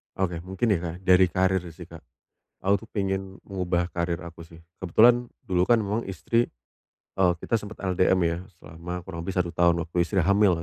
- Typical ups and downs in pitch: No, narrow, 2.3 semitones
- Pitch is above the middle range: No, very low, 95 Hz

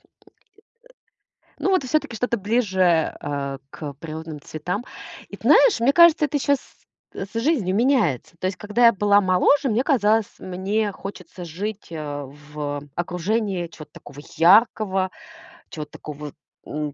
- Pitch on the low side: No, high, 190 Hz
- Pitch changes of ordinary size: No, wide, 6.8 semitones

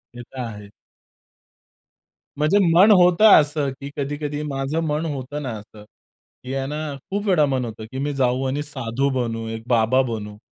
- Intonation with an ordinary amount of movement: Yes, average, 3.6 semitones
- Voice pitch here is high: No, low, 135 Hz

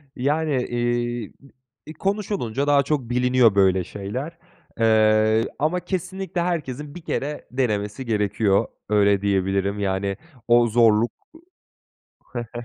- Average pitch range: No, wide, 5.7 semitones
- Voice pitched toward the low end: Yes, low, 120 Hz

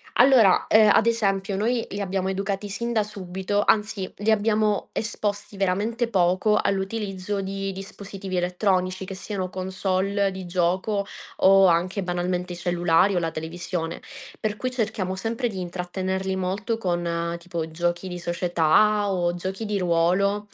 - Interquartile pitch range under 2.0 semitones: No, narrow, 2.5 semitones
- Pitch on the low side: No, high, 190 Hz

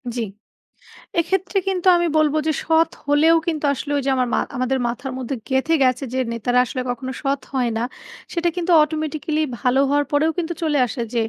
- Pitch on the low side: No, very high, 290 Hz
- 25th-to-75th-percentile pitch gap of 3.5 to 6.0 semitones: Yes, average, 4.1 semitones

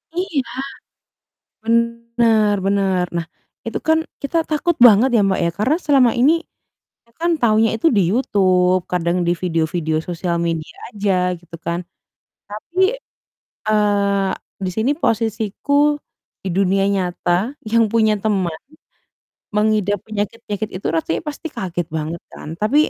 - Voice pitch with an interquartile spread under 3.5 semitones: No, average, 4.3 semitones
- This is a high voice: Yes, high, 205 Hz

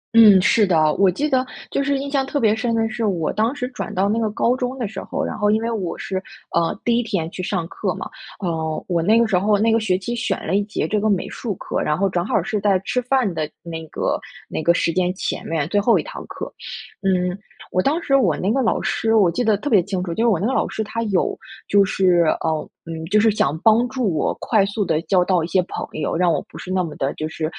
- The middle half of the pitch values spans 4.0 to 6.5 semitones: Yes, average, 4.4 semitones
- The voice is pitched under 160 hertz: No, high, 200 Hz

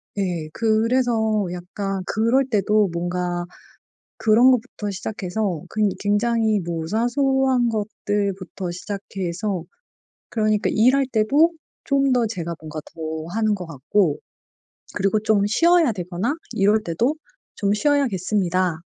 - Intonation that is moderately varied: Yes, average, 4.2 semitones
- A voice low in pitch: No, high, 210 Hz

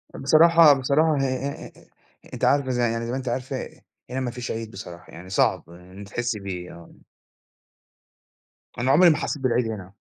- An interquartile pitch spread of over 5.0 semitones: Yes, wide, 5.6 semitones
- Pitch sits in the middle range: No, low, 120 Hz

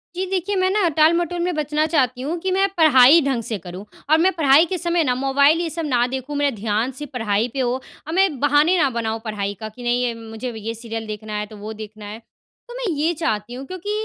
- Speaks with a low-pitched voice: No, very high, 270 Hz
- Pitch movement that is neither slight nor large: No, wide, 6.7 semitones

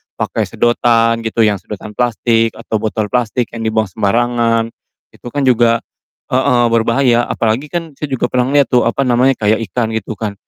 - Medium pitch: No, low, 115 Hz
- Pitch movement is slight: Yes, narrow, 1.8 semitones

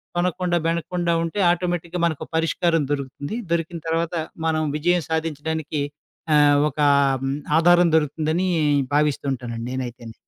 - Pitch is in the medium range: Yes, medium, 160 Hz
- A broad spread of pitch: No, average, 2.9 semitones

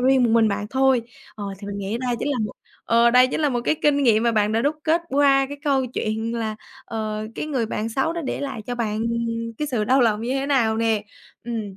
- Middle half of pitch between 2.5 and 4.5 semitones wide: Yes, average, 3.6 semitones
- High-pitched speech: Yes, high, 235 Hz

